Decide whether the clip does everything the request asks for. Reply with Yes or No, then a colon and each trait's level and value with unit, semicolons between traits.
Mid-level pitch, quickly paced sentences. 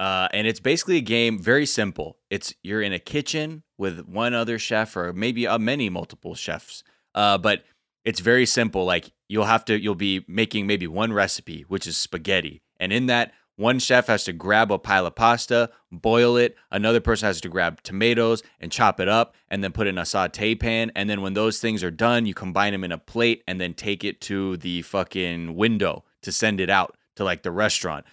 No: low, 105 Hz; fast, 220 wpm